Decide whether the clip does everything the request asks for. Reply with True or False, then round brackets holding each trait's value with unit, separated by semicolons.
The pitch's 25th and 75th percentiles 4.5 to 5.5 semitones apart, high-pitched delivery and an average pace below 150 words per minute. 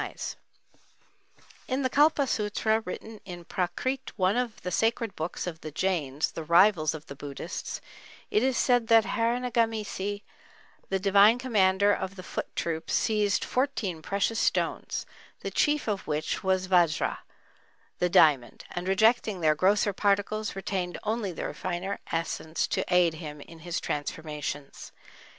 True (4.8 semitones; 195 Hz; 140 wpm)